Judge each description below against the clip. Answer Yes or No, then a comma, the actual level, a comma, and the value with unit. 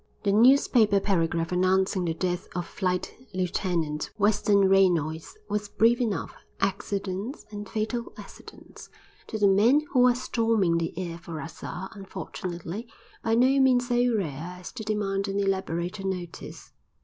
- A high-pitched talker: Yes, high, 195 Hz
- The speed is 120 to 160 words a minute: Yes, average, 145 wpm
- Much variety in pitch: No, average, 3.7 semitones